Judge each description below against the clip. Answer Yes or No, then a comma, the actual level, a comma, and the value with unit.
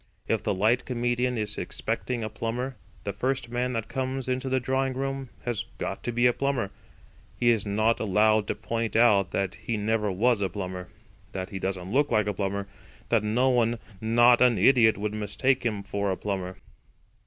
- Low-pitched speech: Yes, low, 115 Hz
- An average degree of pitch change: Yes, average, 3.5 semitones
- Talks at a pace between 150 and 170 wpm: No, average, 190 wpm